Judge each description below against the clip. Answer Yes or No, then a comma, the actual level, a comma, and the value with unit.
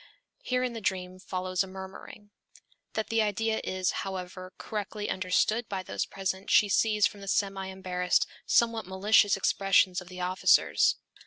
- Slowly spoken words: No, average, 155 wpm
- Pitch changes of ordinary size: No, narrow, 2.3 semitones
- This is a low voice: No, high, 195 Hz